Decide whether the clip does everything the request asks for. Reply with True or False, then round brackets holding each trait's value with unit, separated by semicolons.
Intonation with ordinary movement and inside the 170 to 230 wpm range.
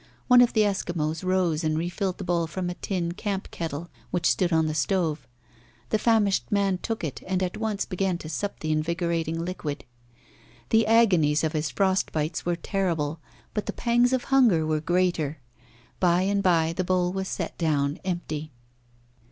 True (3.5 semitones; 180 wpm)